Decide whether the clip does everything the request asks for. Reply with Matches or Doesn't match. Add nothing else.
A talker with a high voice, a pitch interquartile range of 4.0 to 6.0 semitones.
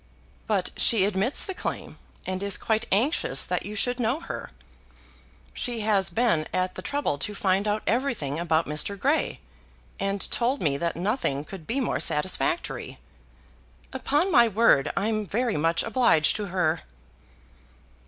Matches